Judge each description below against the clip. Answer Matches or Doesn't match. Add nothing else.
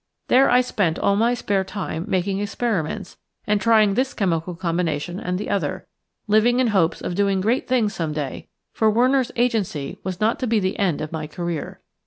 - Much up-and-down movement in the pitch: Doesn't match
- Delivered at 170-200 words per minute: Matches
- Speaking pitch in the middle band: Doesn't match